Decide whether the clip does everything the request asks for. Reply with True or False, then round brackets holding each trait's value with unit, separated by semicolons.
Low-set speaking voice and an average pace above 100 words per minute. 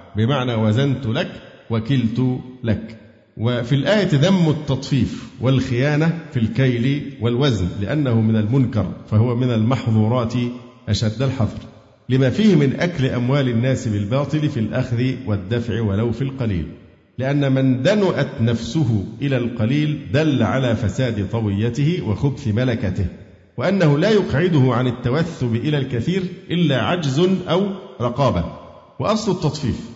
True (125 Hz; 120 wpm)